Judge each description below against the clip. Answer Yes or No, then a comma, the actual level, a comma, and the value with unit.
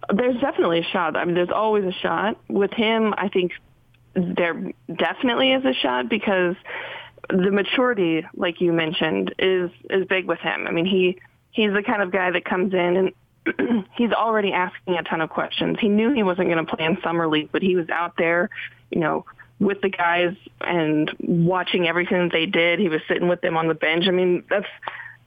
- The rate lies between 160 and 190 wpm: No, average, 200 wpm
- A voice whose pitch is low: No, medium, 180 Hz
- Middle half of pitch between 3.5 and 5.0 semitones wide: No, average, 3.1 semitones